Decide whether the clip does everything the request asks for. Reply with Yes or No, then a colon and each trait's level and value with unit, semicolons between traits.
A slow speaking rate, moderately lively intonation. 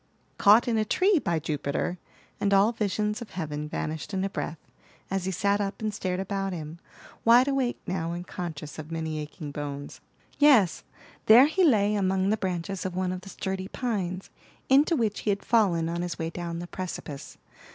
No: average, 190 wpm; average, 4.1 semitones